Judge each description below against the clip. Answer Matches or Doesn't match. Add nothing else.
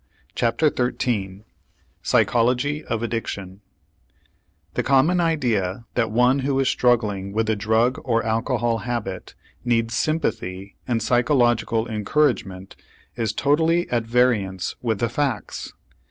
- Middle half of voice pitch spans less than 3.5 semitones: Matches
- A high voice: Doesn't match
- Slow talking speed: Matches